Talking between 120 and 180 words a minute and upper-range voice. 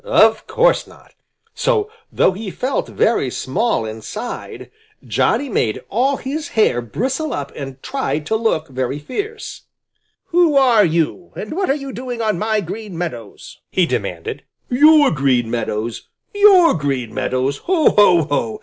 Yes: average, 150 wpm; high, 215 Hz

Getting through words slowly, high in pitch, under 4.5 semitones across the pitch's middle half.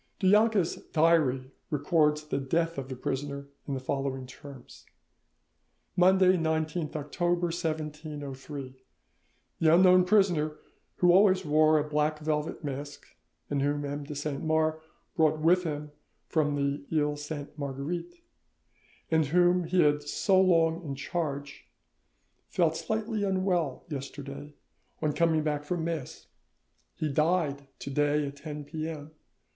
No: slow, 130 wpm; medium, 155 Hz; average, 2.9 semitones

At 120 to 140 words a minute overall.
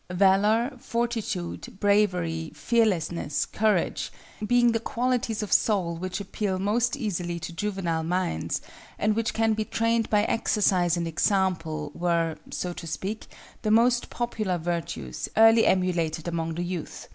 Yes: slow, 135 wpm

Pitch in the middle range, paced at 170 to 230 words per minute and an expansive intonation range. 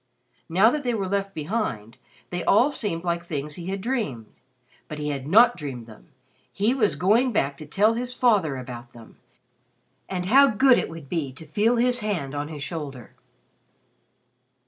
Yes: medium, 180 Hz; average, 175 wpm; wide, 7.5 semitones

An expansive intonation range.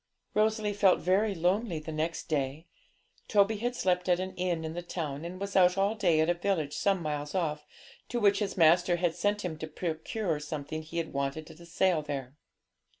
No: average, 3.9 semitones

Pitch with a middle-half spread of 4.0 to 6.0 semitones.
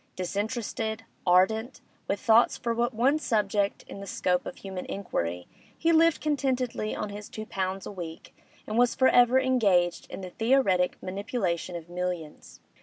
Yes: average, 5.0 semitones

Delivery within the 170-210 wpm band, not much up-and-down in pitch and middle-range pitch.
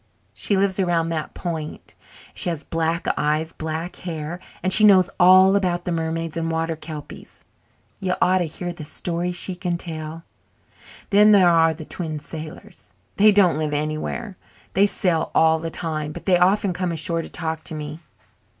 Yes: average, 180 wpm; narrow, 2.3 semitones; medium, 165 Hz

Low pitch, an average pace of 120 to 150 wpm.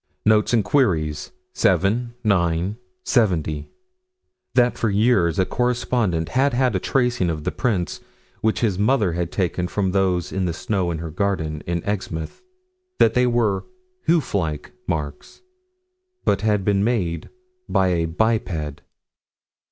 Yes: very low, 95 Hz; average, 140 wpm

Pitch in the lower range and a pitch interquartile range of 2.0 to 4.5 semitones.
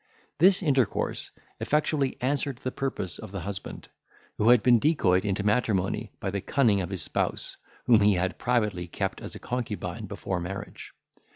No: low, 105 Hz; average, 5.0 semitones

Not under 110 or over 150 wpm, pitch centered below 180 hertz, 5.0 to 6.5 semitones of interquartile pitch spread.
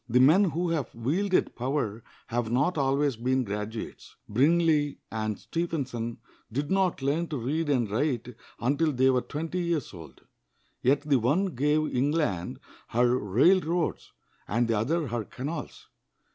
Yes: average, 145 wpm; low, 135 Hz; average, 5.3 semitones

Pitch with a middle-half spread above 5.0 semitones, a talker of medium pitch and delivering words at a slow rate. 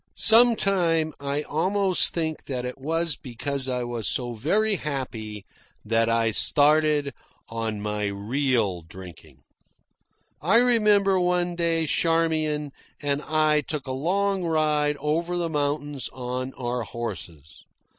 Yes: wide, 5.4 semitones; medium, 145 Hz; slow, 125 wpm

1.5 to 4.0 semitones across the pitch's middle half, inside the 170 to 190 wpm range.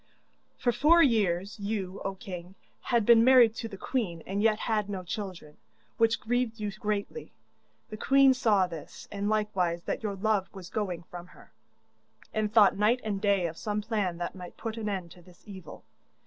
Yes: average, 3.3 semitones; average, 185 wpm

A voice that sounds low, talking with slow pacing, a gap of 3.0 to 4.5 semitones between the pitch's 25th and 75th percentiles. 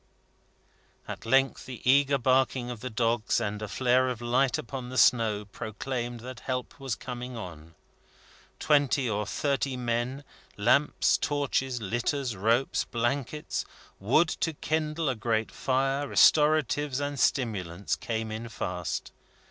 Yes: low, 125 Hz; slow, 130 wpm; average, 3.3 semitones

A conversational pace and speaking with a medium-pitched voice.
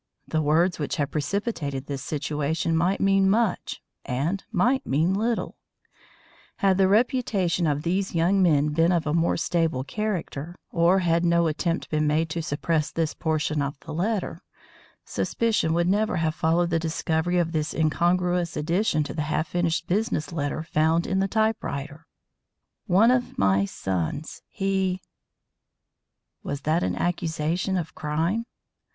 Yes: average, 150 wpm; medium, 165 Hz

